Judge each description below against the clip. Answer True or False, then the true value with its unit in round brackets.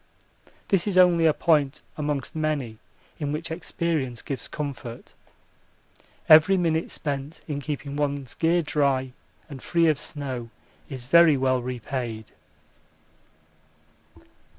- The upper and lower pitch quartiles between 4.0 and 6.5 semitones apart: False (3.6 semitones)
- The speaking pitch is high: False (145 Hz)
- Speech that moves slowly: True (115 wpm)